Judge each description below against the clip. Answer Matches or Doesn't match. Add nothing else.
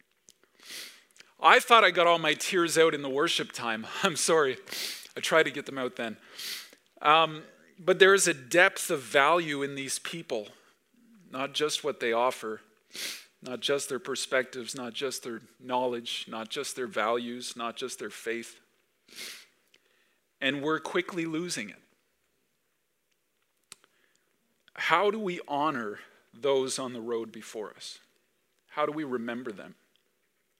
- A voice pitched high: Doesn't match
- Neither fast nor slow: Matches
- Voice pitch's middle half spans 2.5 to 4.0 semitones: Doesn't match